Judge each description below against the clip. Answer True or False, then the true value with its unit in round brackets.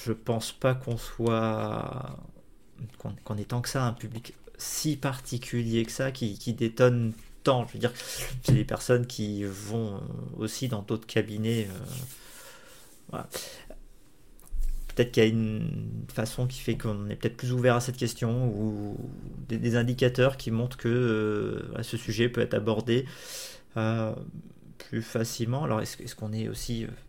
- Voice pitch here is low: True (120 Hz)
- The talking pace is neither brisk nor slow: True (160 wpm)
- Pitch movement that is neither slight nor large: False (2.3 semitones)